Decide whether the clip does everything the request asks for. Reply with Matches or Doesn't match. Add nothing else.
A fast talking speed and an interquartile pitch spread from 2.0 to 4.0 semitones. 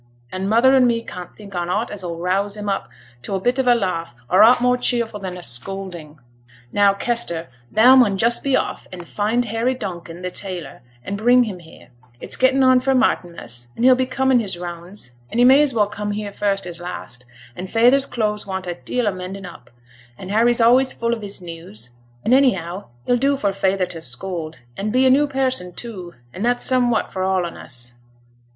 Doesn't match